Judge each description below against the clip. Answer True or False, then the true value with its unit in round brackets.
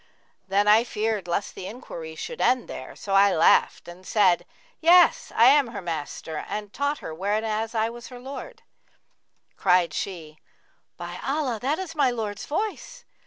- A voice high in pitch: True (215 Hz)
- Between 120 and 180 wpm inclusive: True (165 wpm)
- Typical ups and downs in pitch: False (6.4 semitones)